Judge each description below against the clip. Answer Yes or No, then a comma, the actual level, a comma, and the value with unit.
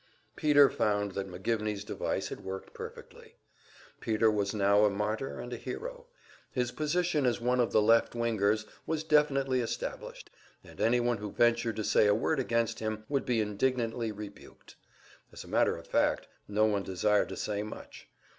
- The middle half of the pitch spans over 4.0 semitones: No, average, 3.3 semitones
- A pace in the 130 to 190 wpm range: Yes, average, 170 wpm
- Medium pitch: No, low, 115 Hz